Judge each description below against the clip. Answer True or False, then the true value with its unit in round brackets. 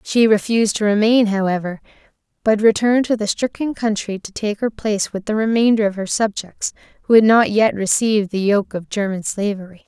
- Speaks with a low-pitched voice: False (210 Hz)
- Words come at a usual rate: True (190 wpm)